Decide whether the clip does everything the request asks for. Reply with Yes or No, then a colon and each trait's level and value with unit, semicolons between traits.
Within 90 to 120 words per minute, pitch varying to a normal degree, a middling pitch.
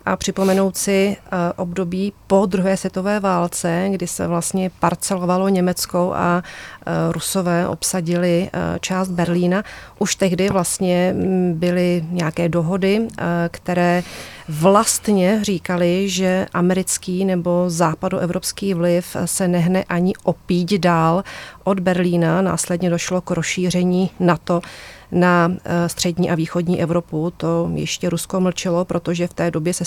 No: slow, 115 wpm; narrow, 1.4 semitones; medium, 180 Hz